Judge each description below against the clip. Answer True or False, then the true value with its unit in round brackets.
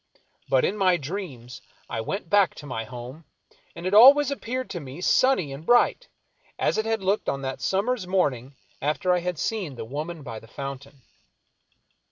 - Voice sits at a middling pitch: True (170 Hz)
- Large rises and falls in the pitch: True (7.1 semitones)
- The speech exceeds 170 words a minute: True (180 wpm)